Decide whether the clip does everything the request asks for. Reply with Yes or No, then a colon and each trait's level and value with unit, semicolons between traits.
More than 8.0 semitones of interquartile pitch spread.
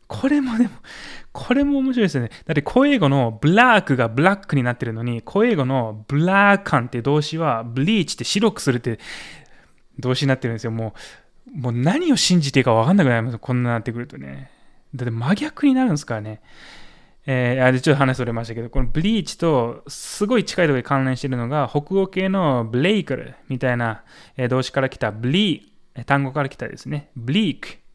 No: wide, 7.6 semitones